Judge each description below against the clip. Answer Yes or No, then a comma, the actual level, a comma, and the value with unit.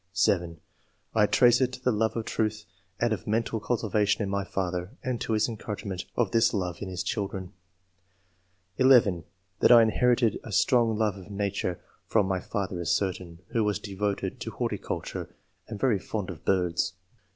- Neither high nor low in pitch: No, low, 105 Hz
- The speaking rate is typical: Yes, average, 175 wpm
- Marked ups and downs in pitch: No, average, 3.3 semitones